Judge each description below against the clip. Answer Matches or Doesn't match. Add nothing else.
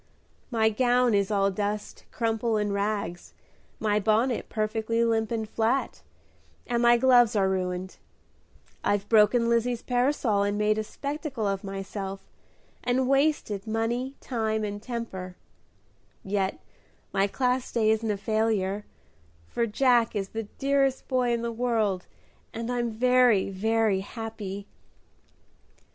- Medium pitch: Doesn't match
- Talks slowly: Matches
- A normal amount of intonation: Matches